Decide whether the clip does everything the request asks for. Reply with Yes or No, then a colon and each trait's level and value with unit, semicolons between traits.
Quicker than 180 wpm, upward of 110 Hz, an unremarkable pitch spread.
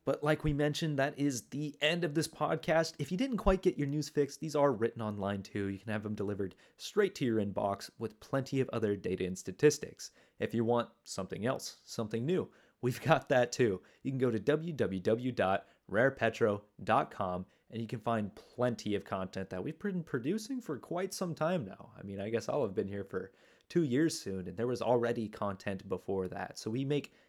No: fast, 205 wpm; low, 125 Hz; wide, 6.6 semitones